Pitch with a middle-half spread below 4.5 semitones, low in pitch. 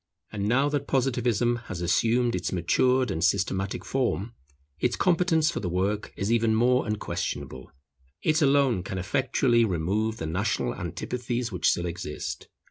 No: average, 5.1 semitones; low, 115 Hz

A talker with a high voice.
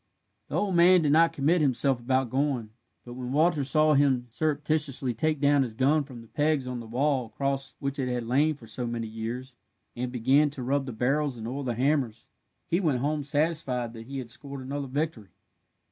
No: low, 135 Hz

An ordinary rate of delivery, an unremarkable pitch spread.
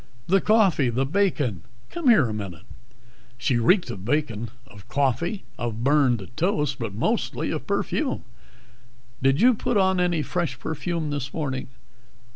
No: average, 145 wpm; wide, 6.9 semitones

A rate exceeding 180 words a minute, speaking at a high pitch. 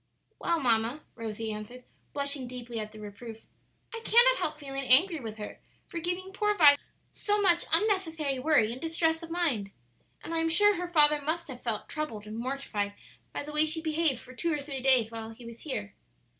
Yes: average, 200 wpm; very high, 285 Hz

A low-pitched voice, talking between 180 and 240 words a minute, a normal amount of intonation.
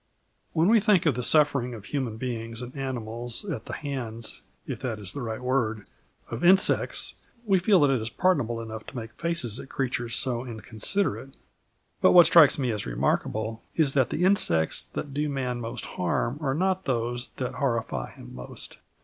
Yes: low, 125 Hz; average, 185 wpm; average, 4.5 semitones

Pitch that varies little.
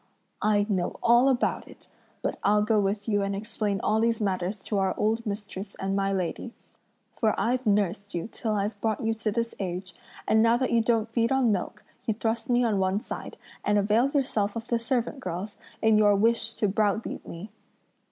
Yes: narrow, 2.3 semitones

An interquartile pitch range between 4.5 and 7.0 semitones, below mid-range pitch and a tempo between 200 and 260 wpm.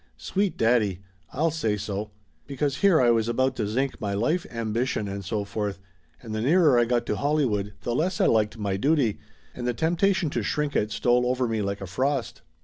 Yes: average, 5.1 semitones; low, 120 Hz; fast, 205 wpm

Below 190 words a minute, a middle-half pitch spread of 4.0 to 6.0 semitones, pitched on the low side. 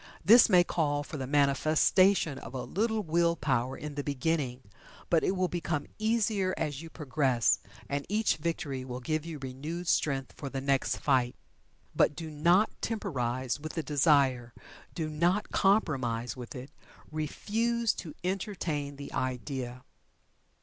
No: average, 150 wpm; average, 4.8 semitones; medium, 150 Hz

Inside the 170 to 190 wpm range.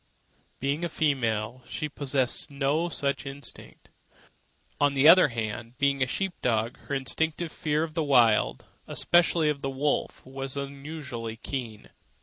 No: average, 145 wpm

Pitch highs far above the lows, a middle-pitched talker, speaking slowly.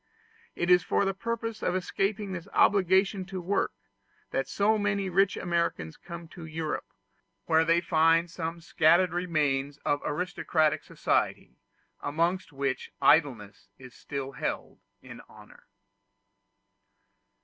No: average, 3.6 semitones; medium, 170 Hz; slow, 125 wpm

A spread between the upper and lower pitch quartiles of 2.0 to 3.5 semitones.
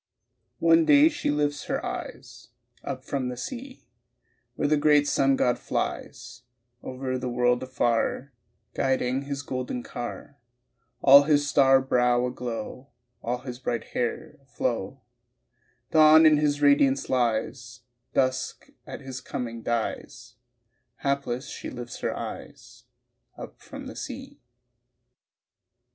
Yes: average, 2.7 semitones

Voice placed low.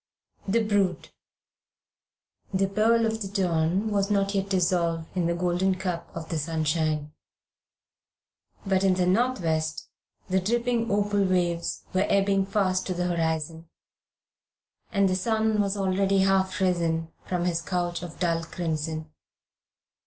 No: medium, 185 Hz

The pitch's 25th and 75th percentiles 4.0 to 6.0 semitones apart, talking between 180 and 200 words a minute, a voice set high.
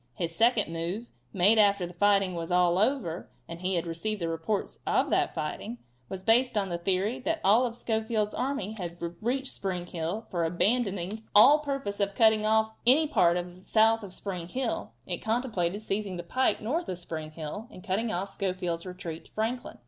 Yes: average, 4.3 semitones; average, 185 wpm; high, 200 Hz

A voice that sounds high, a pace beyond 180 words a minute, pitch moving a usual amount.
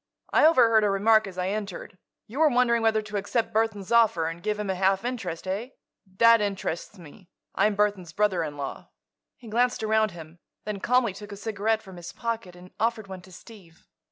Yes: high, 210 Hz; average, 200 wpm; average, 3.3 semitones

